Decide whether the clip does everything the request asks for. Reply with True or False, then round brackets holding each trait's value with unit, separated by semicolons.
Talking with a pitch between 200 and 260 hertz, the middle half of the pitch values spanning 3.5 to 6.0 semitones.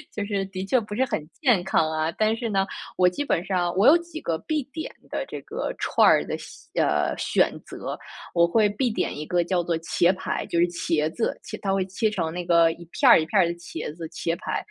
False (185 Hz; 4.2 semitones)